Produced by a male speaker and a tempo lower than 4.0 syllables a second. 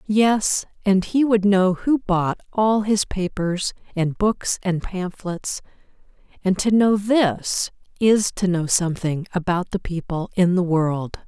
No: female; 3.6 syllables/s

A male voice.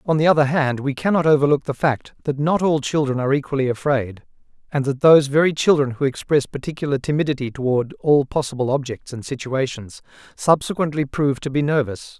Yes: male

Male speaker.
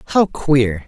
Yes: male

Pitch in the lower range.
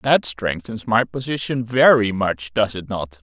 Yes: low, 115 Hz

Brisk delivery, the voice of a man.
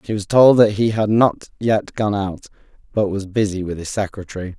Yes: fast, 210 wpm; male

